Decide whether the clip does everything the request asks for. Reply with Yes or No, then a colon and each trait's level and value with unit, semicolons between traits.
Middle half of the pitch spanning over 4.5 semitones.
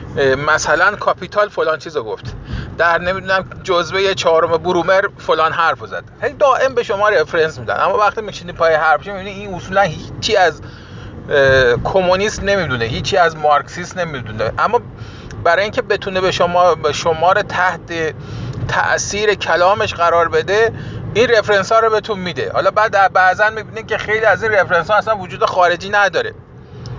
No: average, 4.2 semitones